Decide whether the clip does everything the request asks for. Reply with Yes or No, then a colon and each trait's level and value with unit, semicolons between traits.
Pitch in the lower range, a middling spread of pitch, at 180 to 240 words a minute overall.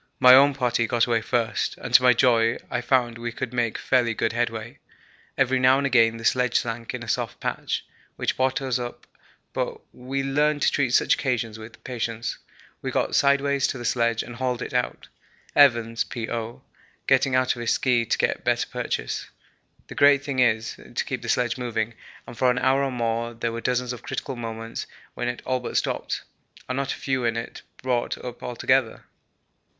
No: low, 120 Hz; narrow, 1.9 semitones; average, 195 wpm